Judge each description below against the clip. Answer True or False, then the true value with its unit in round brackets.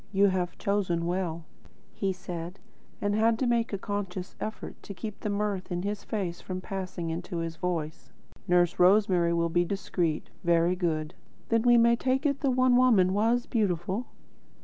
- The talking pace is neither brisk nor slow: True (170 wpm)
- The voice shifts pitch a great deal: False (3.8 semitones)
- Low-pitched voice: False (190 Hz)